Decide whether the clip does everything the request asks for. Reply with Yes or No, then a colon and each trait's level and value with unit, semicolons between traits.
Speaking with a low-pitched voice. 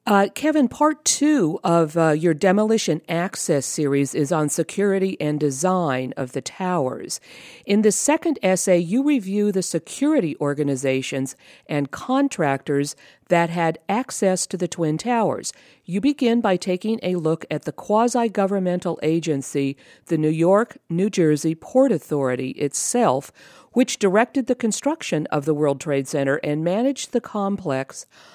No: medium, 180 Hz